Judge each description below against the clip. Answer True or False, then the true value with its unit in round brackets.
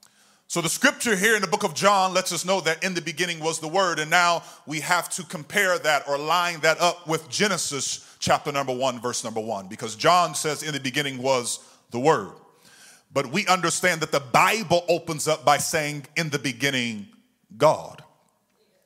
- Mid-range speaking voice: True (165 Hz)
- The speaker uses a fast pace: False (195 wpm)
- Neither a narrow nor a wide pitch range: True (4.1 semitones)